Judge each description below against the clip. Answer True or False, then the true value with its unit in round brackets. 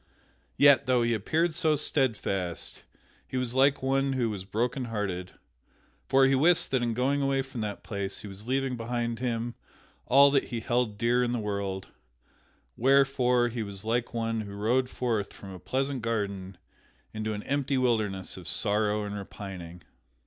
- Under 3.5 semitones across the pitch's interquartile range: False (4.3 semitones)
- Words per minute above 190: False (165 wpm)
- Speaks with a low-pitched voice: True (120 Hz)